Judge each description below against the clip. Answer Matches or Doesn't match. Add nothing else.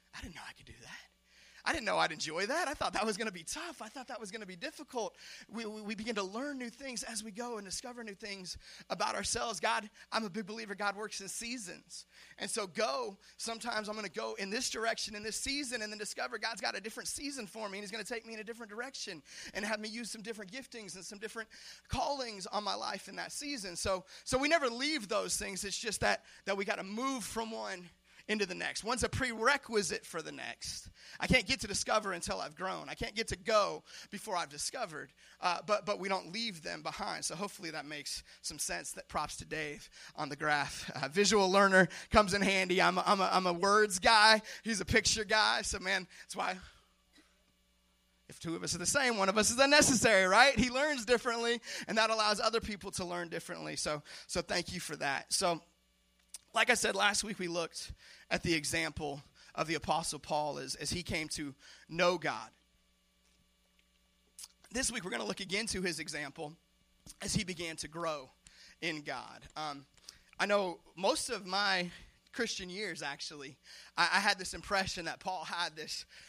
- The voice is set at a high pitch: Matches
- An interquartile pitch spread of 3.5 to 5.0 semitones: Matches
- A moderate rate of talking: Doesn't match